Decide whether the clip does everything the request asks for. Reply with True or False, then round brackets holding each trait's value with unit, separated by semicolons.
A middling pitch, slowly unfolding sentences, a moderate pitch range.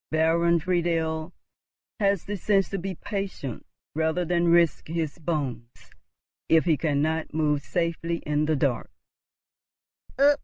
False (165 Hz; 120 wpm; 2.1 semitones)